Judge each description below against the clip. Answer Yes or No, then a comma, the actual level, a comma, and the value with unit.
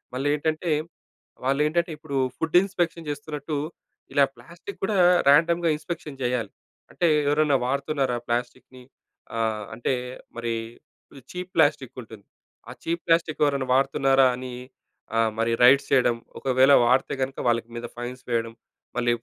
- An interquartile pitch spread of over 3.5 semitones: Yes, average, 4.2 semitones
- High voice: No, low, 135 Hz